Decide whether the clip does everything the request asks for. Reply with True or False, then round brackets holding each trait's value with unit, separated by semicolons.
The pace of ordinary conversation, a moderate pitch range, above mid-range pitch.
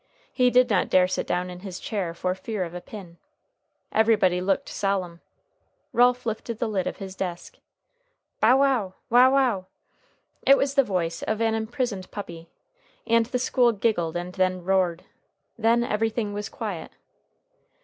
True (160 wpm; 4.4 semitones; 205 Hz)